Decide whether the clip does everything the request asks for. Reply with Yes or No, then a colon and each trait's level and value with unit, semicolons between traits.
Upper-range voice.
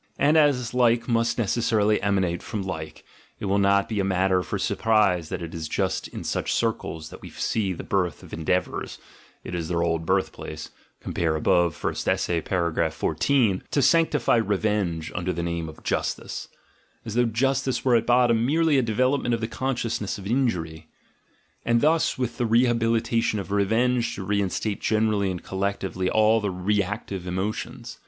No: low, 105 Hz